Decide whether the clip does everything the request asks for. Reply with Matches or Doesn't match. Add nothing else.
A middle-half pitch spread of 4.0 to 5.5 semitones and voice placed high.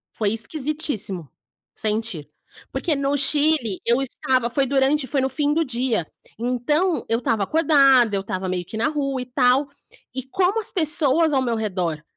Matches